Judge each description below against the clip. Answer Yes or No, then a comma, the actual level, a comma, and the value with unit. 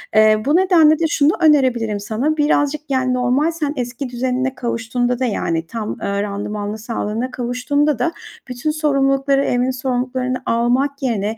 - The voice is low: No, very high, 255 Hz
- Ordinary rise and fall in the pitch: Yes, average, 3.5 semitones